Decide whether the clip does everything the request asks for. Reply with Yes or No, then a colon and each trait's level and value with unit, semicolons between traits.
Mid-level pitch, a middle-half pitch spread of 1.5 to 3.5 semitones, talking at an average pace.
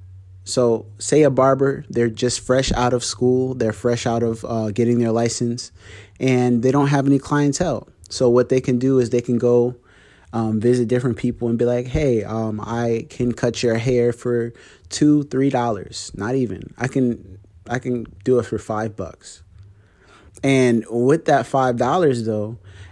No: low, 120 Hz; average, 2.8 semitones; average, 180 wpm